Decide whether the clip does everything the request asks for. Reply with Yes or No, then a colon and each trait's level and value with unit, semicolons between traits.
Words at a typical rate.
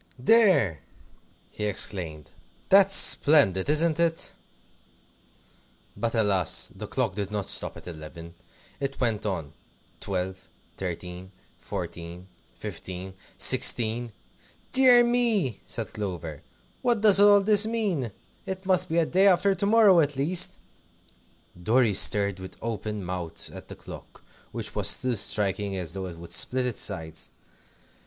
No: slow, 130 wpm